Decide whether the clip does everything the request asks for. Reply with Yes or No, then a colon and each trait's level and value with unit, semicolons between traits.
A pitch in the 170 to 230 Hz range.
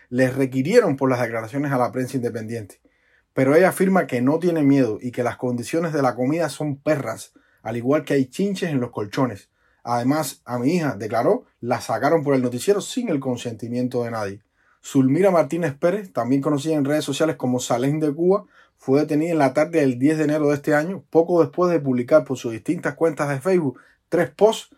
No: medium, 140 Hz